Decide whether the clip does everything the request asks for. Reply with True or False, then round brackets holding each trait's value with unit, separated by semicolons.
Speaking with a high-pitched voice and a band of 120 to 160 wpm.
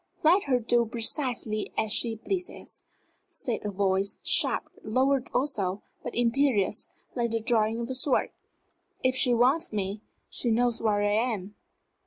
True (235 Hz; 150 wpm)